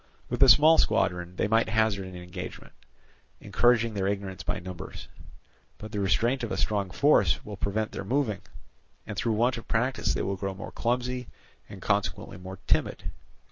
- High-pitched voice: No, low, 105 Hz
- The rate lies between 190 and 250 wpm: No, average, 175 wpm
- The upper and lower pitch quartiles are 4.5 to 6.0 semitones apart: No, average, 3.9 semitones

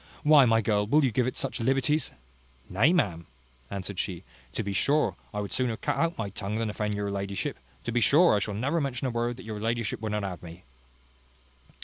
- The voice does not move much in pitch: No, average, 4.5 semitones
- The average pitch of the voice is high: No, low, 110 Hz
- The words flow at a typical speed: No, fast, 220 wpm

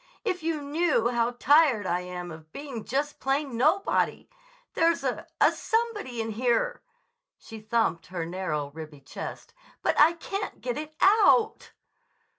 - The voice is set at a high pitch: Yes, very high, 270 Hz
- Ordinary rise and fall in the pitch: No, wide, 8.5 semitones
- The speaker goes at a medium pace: No, slow, 130 wpm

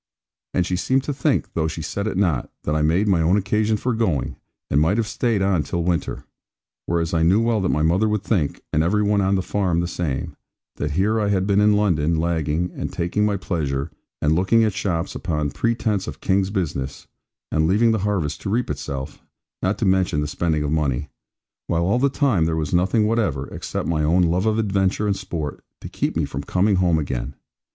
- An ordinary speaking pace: No, fast, 220 wpm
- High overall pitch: No, very low, 90 Hz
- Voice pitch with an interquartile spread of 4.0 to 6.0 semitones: Yes, average, 4.7 semitones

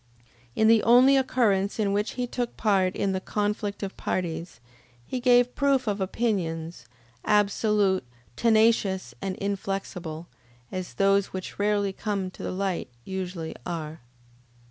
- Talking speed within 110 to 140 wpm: Yes, slow, 135 wpm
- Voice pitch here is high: Yes, high, 200 Hz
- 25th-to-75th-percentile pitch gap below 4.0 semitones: Yes, average, 2.8 semitones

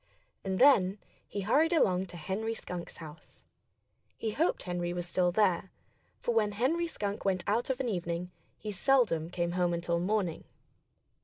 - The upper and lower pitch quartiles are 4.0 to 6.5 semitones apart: Yes, average, 4.3 semitones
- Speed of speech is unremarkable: Yes, average, 160 wpm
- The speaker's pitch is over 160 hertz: Yes, high, 190 Hz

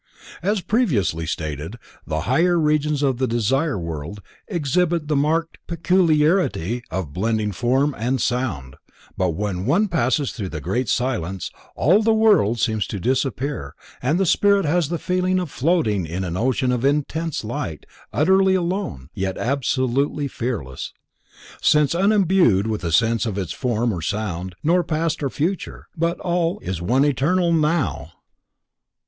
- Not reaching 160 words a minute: Yes, average, 150 wpm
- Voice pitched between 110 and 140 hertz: Yes, low, 135 Hz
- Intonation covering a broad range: Yes, wide, 8.4 semitones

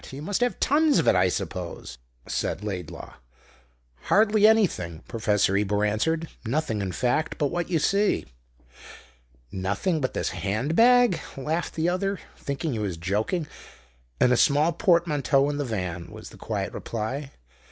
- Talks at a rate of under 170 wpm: Yes, average, 150 wpm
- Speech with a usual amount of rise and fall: No, wide, 8.9 semitones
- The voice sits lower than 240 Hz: Yes, medium, 140 Hz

